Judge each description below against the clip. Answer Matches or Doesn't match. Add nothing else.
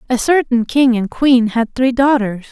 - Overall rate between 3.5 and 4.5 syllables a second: Matches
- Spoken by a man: Doesn't match